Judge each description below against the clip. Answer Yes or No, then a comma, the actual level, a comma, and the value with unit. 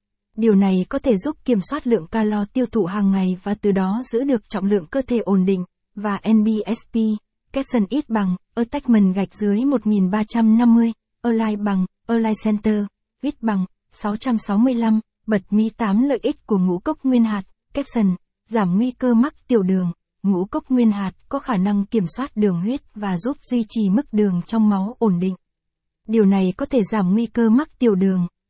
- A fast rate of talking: No, average, 185 wpm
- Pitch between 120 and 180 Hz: No, high, 215 Hz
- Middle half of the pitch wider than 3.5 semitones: No, average, 3.2 semitones